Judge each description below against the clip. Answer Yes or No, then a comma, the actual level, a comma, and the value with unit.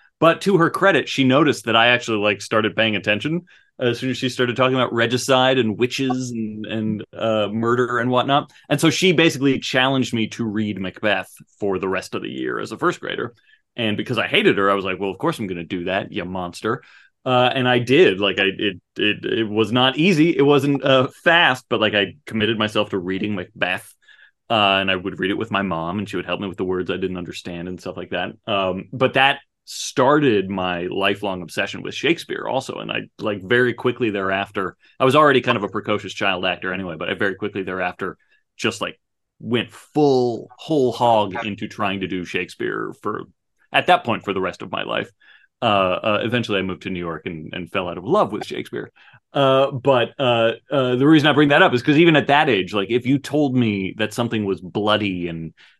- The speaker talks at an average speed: No, fast, 225 wpm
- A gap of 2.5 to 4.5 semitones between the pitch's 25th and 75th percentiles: No, average, 4.9 semitones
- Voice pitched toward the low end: Yes, low, 110 Hz